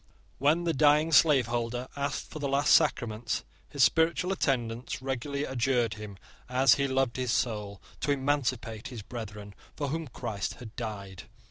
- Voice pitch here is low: Yes, low, 125 Hz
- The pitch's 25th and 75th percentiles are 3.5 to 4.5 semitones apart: Yes, average, 3.8 semitones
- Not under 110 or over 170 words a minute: Yes, average, 150 wpm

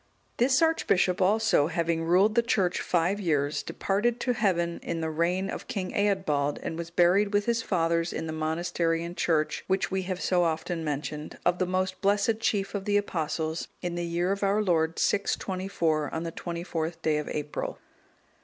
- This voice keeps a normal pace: Yes, average, 180 wpm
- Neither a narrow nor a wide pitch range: Yes, average, 3.3 semitones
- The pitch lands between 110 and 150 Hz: No, medium, 175 Hz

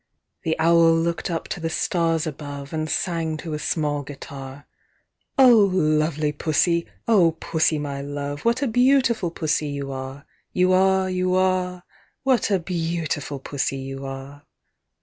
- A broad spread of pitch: No, average, 4.1 semitones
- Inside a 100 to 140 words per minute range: No, average, 150 wpm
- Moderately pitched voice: Yes, medium, 160 Hz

